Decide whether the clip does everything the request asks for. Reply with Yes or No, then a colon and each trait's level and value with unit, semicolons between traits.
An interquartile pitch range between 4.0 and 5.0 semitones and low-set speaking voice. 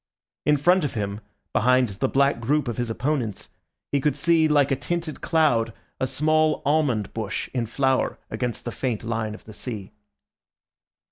Yes: average, 4.7 semitones; low, 130 Hz